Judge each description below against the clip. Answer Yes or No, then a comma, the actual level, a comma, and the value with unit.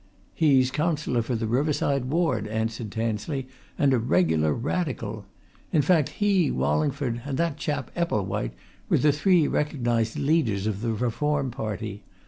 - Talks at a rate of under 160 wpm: Yes, average, 140 wpm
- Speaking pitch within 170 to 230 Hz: No, low, 130 Hz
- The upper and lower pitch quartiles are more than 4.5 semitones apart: Yes, average, 5.1 semitones